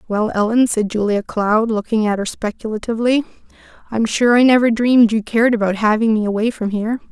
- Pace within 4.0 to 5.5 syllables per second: No, 6.0 syllables/s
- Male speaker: No, female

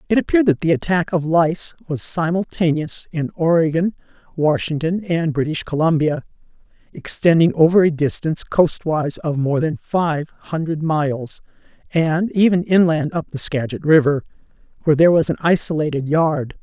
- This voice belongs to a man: No, female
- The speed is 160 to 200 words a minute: No, average, 140 wpm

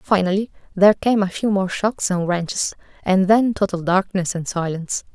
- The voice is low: No, high, 190 Hz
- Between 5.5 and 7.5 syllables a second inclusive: No, 5.1 syllables/s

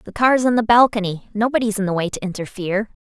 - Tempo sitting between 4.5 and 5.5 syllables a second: No, 6.3 syllables/s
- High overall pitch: Yes, high, 210 Hz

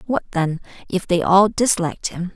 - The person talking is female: Yes, female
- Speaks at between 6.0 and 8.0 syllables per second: No, 4.9 syllables/s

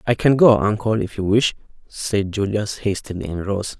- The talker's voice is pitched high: No, low, 105 Hz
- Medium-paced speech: Yes, average, 190 wpm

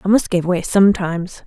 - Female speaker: Yes, female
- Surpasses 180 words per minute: Yes, fast, 205 wpm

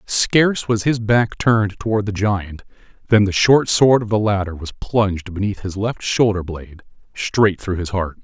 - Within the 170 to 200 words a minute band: Yes, average, 190 wpm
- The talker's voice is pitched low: Yes, low, 105 Hz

